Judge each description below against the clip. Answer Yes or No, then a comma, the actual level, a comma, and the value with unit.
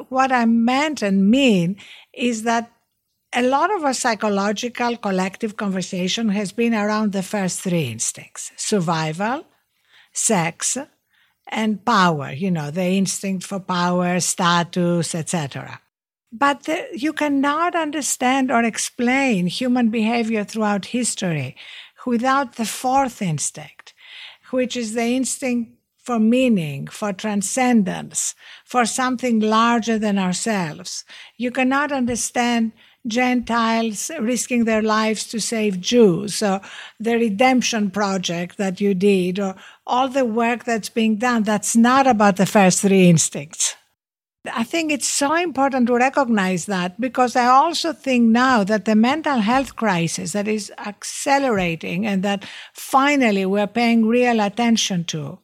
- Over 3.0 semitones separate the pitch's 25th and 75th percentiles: Yes, average, 4.3 semitones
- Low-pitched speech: No, high, 225 Hz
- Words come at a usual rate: No, slow, 130 wpm